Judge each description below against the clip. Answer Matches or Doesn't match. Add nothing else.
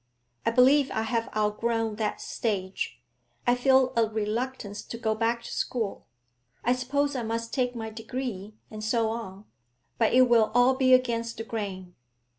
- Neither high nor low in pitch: Doesn't match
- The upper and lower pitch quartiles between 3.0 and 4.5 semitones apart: Doesn't match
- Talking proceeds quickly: Doesn't match